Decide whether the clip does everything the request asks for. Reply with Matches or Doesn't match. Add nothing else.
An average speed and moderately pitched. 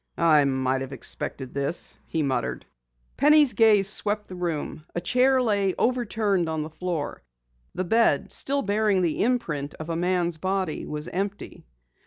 Matches